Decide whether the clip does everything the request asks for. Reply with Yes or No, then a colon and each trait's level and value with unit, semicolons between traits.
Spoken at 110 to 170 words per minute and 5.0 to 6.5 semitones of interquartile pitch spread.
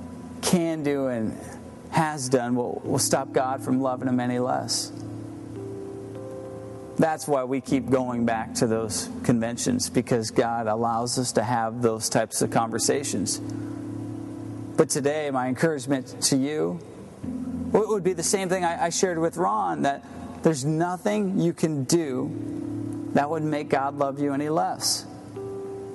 Yes: average, 150 wpm; average, 5.3 semitones